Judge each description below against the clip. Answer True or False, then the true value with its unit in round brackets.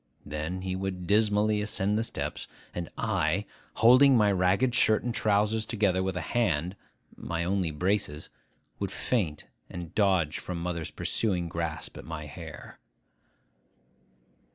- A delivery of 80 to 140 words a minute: True (135 wpm)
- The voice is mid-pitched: False (95 Hz)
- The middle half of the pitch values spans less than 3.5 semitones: False (3.9 semitones)